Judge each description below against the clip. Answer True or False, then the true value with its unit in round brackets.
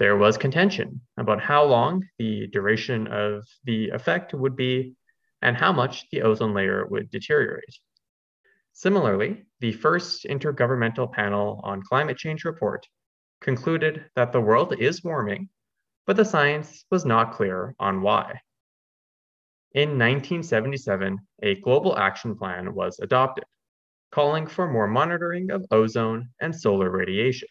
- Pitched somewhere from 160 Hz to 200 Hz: False (135 Hz)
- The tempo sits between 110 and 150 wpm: True (135 wpm)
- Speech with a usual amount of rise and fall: False (7.6 semitones)